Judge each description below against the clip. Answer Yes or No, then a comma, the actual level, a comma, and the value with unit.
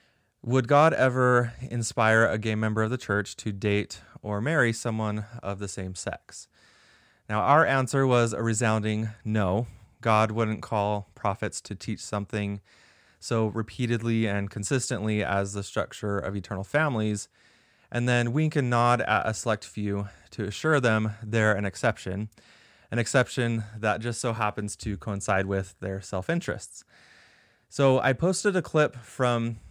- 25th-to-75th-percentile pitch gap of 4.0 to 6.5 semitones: No, average, 2.8 semitones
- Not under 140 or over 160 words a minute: Yes, average, 155 wpm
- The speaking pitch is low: Yes, low, 110 Hz